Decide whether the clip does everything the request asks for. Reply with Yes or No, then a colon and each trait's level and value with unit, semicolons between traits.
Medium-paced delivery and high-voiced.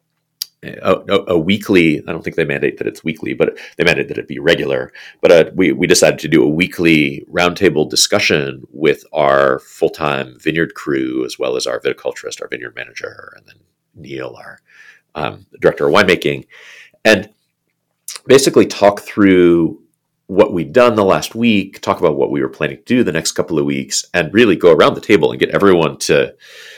Yes: average, 190 wpm; very high, 360 Hz